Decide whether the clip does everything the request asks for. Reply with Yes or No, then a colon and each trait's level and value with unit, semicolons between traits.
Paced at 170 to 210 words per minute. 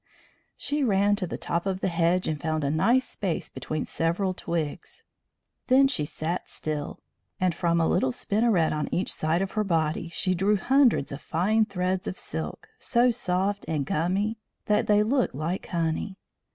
Yes: average, 175 wpm